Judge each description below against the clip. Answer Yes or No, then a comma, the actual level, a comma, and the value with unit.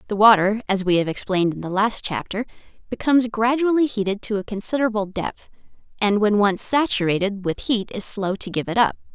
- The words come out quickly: No, average, 190 wpm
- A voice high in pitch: Yes, high, 210 Hz